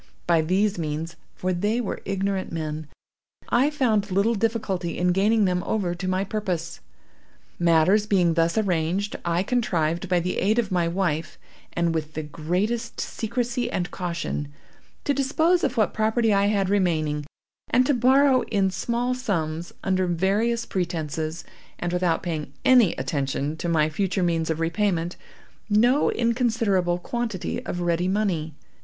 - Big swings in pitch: No, average, 4.5 semitones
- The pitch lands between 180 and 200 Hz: Yes, medium, 185 Hz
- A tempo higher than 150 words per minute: No, average, 145 wpm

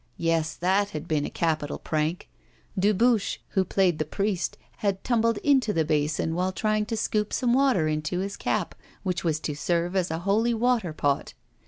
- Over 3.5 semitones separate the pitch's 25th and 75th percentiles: Yes, average, 5.1 semitones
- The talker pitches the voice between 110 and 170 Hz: No, medium, 185 Hz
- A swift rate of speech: No, average, 180 wpm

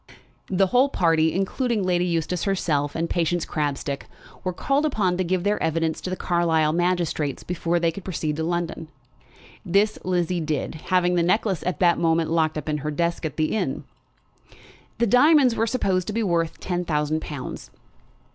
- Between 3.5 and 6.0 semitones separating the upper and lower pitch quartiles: No, average, 2.7 semitones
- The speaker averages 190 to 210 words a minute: No, average, 175 wpm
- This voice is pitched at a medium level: Yes, medium, 175 Hz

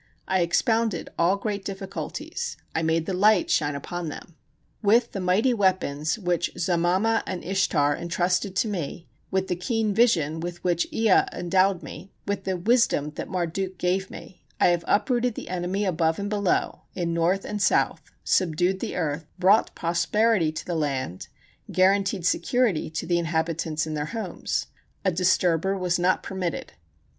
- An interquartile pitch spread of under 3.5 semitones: Yes, average, 2.9 semitones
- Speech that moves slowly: No, average, 160 wpm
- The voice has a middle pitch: Yes, medium, 180 Hz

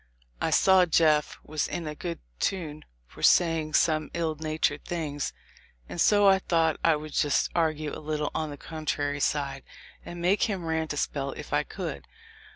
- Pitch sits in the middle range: Yes, medium, 155 Hz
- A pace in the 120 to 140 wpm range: No, average, 175 wpm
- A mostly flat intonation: Yes, narrow, 2.2 semitones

